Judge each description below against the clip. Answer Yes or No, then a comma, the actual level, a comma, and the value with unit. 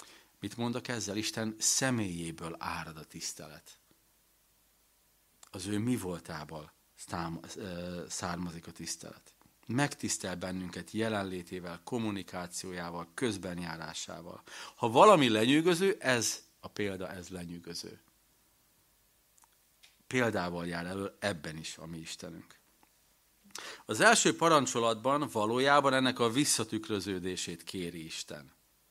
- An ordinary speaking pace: No, slow, 95 wpm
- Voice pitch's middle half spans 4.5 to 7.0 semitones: Yes, average, 5.0 semitones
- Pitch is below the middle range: Yes, very low, 95 Hz